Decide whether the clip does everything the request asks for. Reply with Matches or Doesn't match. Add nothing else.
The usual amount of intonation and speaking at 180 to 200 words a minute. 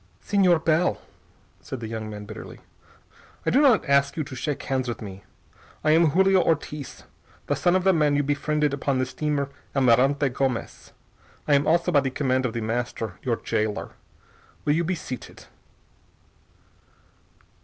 Doesn't match